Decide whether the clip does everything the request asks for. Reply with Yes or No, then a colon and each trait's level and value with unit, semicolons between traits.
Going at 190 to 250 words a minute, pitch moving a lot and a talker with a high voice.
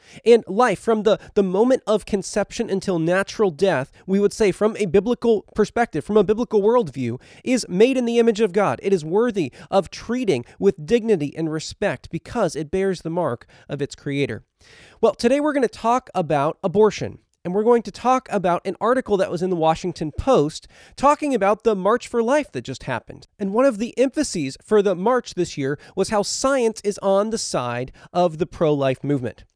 Yes: average, 200 wpm; wide, 5.8 semitones; high, 200 Hz